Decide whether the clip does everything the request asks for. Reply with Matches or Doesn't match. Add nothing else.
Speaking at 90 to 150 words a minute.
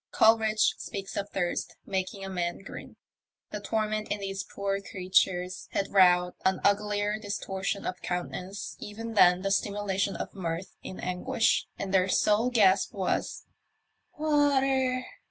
Matches